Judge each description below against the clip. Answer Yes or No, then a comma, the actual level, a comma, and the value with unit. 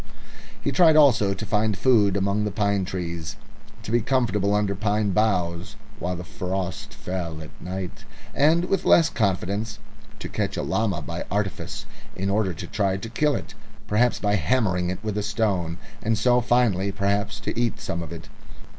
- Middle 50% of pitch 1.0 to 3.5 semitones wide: Yes, average, 2.9 semitones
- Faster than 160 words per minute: Yes, average, 175 wpm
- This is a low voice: Yes, low, 100 Hz